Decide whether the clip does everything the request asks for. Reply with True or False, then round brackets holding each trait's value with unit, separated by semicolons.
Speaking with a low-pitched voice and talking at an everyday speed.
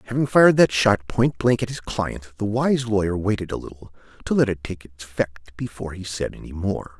False (105 Hz; 215 wpm)